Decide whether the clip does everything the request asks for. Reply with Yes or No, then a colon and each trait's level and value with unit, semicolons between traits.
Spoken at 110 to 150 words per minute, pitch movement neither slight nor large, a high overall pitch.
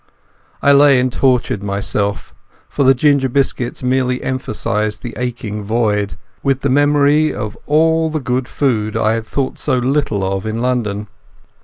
No: average, 145 wpm; average, 4.5 semitones; low, 125 Hz